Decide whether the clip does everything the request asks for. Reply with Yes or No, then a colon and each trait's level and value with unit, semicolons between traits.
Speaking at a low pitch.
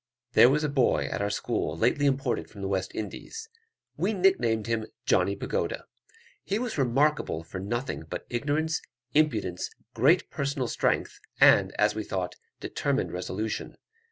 Yes: low, 120 Hz